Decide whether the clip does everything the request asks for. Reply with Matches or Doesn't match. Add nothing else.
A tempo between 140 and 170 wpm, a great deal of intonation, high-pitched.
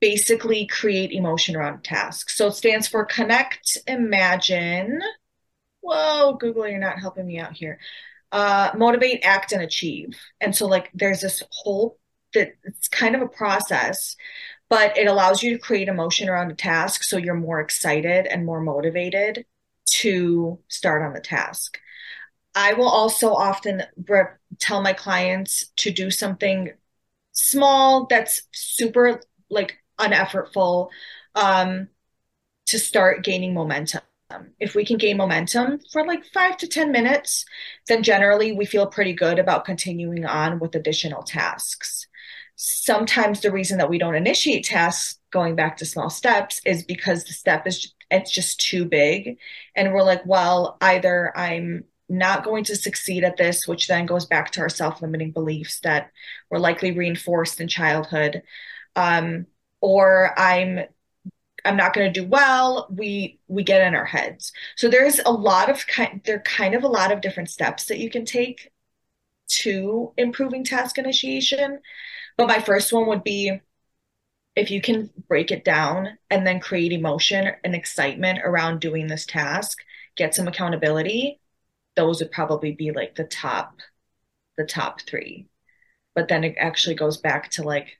Doesn't match